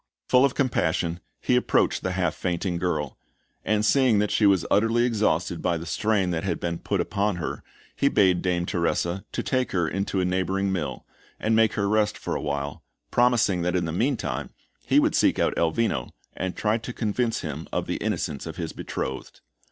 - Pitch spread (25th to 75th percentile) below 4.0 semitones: No, average, 4.3 semitones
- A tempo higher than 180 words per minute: Yes, average, 195 wpm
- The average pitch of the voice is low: Yes, very low, 95 Hz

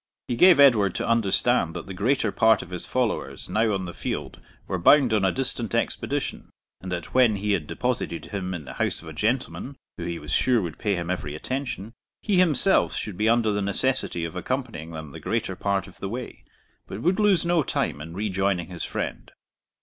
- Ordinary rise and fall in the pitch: No, wide, 5.9 semitones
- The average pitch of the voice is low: Yes, low, 105 Hz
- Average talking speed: No, fast, 210 wpm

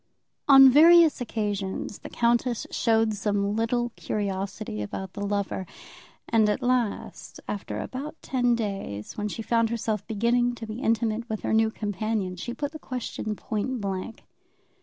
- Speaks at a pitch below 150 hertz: No, high, 220 Hz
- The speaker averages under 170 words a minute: Yes, average, 150 wpm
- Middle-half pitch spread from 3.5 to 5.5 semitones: No, average, 2.9 semitones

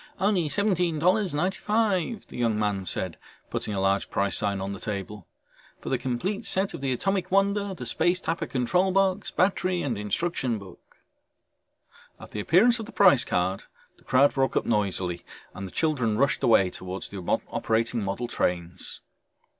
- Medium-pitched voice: No, low, 130 Hz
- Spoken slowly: No, average, 165 wpm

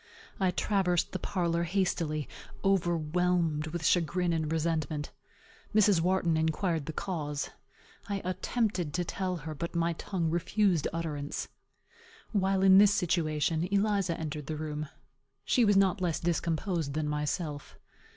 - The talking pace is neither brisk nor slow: No, slow, 130 wpm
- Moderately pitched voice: Yes, medium, 170 Hz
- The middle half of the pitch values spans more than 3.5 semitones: No, average, 3.1 semitones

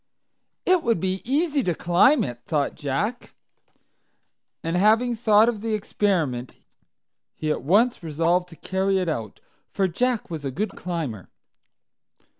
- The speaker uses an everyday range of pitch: No, wide, 6.0 semitones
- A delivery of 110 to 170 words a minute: Yes, average, 140 wpm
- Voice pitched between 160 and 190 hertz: Yes, medium, 185 Hz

